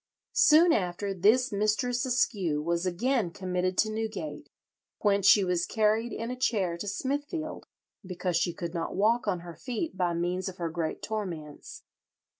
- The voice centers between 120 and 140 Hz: No, high, 200 Hz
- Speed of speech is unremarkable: Yes, average, 160 wpm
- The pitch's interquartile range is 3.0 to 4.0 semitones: No, average, 4.7 semitones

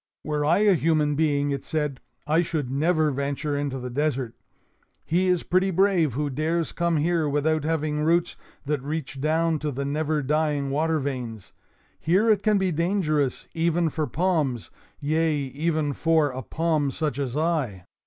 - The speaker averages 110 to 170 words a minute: Yes, average, 165 wpm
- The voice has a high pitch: No, medium, 155 Hz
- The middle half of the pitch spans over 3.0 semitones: No, narrow, 2.6 semitones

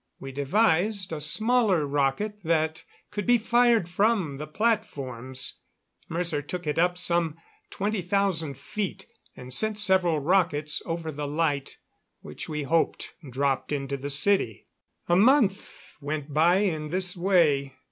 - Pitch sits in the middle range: Yes, medium, 165 Hz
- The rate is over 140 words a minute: No, slow, 135 wpm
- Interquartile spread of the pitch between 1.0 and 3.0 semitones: No, average, 5.3 semitones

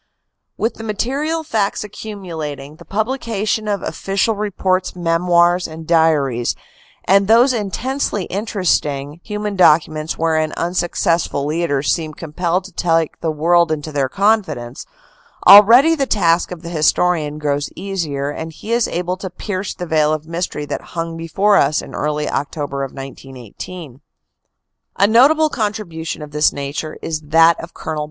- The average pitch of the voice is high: No, medium, 170 Hz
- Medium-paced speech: Yes, average, 145 wpm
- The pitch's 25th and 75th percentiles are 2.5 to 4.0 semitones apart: No, average, 4.8 semitones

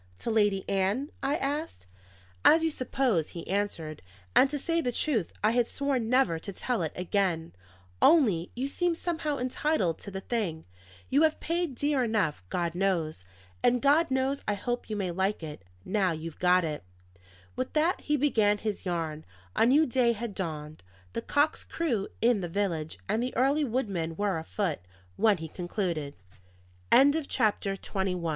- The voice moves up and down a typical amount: No, wide, 7.4 semitones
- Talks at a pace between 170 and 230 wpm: Yes, average, 175 wpm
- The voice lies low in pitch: No, high, 210 Hz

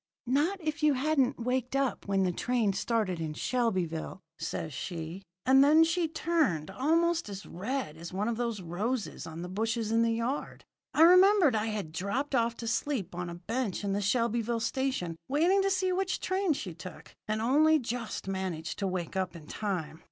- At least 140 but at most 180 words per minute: No, average, 190 wpm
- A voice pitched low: No, high, 230 Hz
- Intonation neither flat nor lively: No, wide, 7.0 semitones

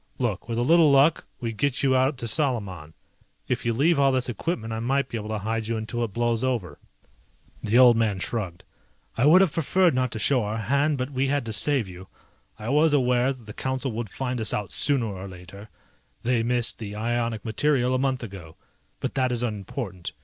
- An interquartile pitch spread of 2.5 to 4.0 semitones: Yes, average, 3.7 semitones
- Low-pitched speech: Yes, low, 120 Hz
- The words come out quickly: Yes, fast, 215 wpm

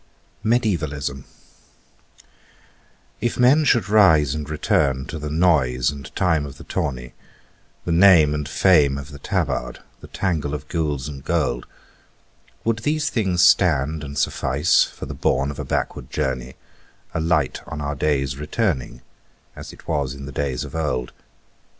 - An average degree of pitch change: Yes, average, 4.3 semitones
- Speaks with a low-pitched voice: Yes, very low, 75 Hz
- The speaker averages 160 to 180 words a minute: No, average, 150 wpm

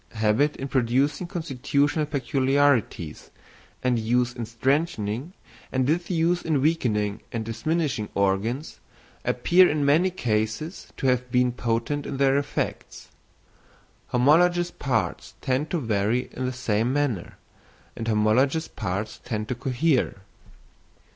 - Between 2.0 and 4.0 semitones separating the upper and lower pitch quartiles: No, average, 4.5 semitones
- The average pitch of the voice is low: Yes, low, 130 Hz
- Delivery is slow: Yes, slow, 120 wpm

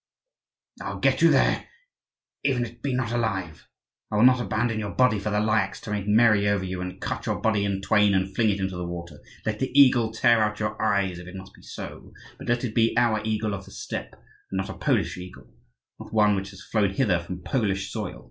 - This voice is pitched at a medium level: No, low, 105 Hz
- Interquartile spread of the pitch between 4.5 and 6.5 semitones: No, average, 2.9 semitones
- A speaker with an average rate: No, fast, 235 wpm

